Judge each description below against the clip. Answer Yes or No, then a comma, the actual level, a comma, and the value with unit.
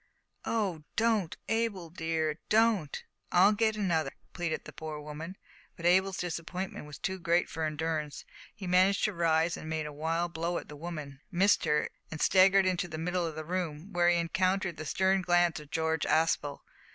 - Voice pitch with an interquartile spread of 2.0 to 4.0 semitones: Yes, average, 3.0 semitones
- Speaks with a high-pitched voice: No, medium, 170 Hz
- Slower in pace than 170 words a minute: No, average, 180 wpm